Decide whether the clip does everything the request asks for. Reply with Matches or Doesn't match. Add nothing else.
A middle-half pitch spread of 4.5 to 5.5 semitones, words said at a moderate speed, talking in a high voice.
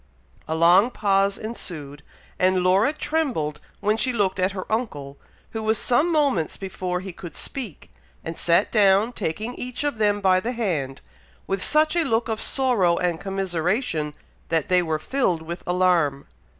Matches